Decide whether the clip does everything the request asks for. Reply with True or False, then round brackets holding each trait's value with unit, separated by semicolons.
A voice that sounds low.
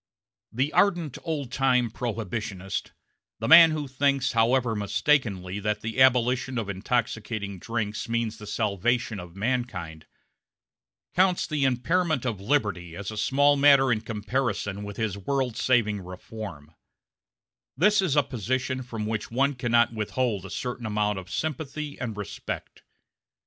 True (120 Hz)